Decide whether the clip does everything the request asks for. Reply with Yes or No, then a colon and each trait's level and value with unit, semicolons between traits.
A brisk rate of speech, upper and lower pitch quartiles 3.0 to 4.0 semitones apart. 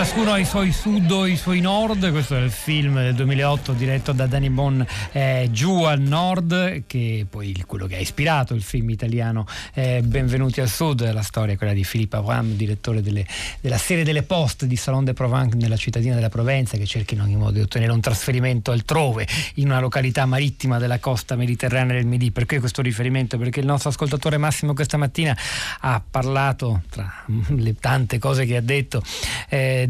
Yes: fast, 195 wpm; average, 3.7 semitones